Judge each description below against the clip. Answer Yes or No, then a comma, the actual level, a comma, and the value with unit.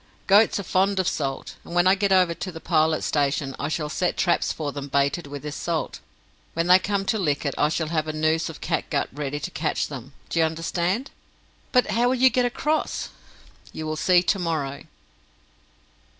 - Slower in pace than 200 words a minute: No, fast, 205 wpm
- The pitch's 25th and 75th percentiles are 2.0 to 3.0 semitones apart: No, average, 4.0 semitones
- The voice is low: No, medium, 165 Hz